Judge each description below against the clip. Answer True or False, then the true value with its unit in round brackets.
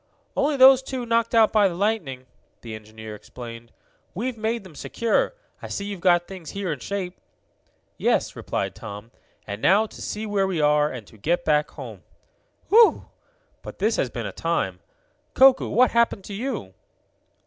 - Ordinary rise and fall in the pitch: False (7.7 semitones)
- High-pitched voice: True (195 Hz)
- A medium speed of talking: True (170 wpm)